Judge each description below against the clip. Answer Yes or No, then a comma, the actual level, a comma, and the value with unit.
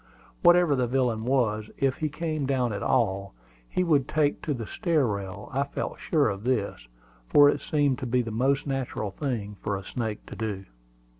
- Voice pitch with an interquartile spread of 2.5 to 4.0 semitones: No, average, 5.1 semitones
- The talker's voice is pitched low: Yes, low, 125 Hz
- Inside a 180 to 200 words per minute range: Yes, average, 195 wpm